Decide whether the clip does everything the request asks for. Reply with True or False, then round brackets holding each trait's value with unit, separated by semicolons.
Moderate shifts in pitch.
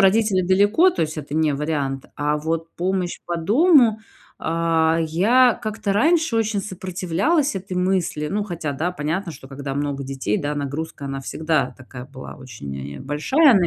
False (5.7 semitones)